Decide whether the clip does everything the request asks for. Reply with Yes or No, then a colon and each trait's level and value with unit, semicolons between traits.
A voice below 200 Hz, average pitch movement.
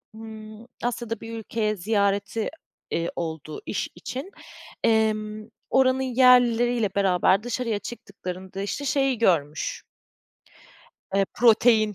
No: high, 220 Hz; average, 3.2 semitones